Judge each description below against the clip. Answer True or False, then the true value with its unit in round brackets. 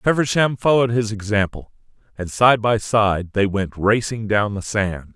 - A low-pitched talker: True (110 Hz)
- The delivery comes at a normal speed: True (165 wpm)